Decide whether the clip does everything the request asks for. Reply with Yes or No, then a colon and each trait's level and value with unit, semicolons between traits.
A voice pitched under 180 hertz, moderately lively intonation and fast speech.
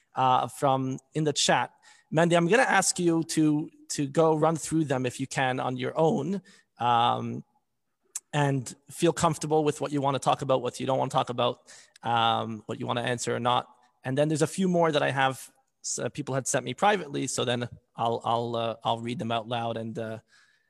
Yes: low, 135 Hz; average, 4.8 semitones; fast, 220 wpm